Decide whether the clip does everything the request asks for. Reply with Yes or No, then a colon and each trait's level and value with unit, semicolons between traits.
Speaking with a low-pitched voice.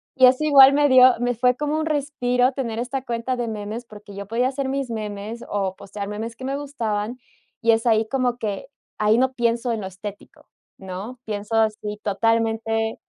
No: high, 230 Hz